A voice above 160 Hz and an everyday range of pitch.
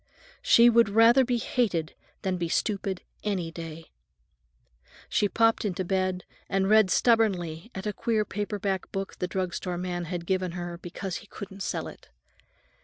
Yes: high, 190 Hz; average, 3.4 semitones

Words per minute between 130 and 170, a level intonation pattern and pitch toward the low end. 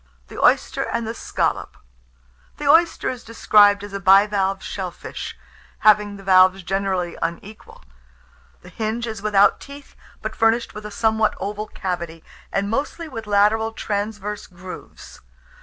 No: average, 140 wpm; narrow, 2.3 semitones; high, 205 Hz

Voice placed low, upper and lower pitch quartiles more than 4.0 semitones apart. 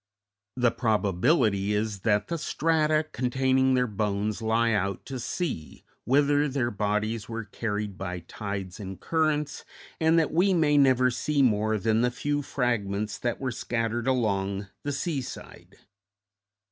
Yes: low, 115 Hz; average, 5.1 semitones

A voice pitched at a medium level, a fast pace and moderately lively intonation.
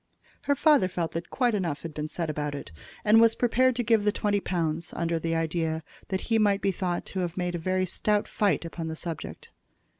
Yes: medium, 180 Hz; fast, 215 wpm; average, 4.2 semitones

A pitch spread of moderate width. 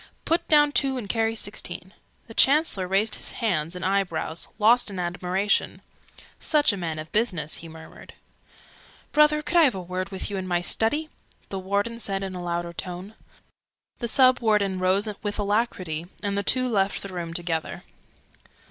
Yes: average, 4.3 semitones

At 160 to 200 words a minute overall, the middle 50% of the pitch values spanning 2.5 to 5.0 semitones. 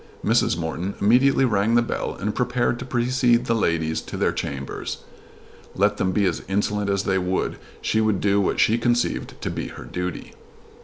Yes: average, 185 wpm; average, 4.1 semitones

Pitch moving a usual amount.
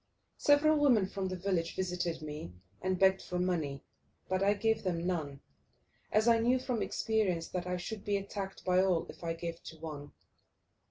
Yes: average, 3.6 semitones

